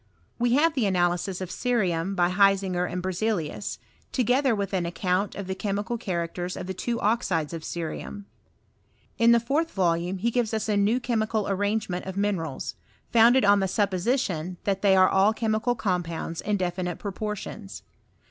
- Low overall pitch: No, high, 195 Hz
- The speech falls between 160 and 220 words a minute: Yes, average, 165 wpm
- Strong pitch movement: No, average, 3.6 semitones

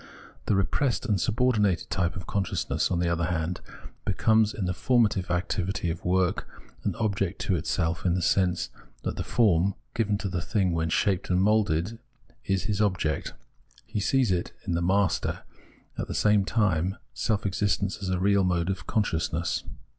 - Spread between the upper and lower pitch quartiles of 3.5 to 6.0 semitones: No, average, 3.0 semitones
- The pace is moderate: Yes, average, 170 wpm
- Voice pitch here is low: Yes, very low, 95 Hz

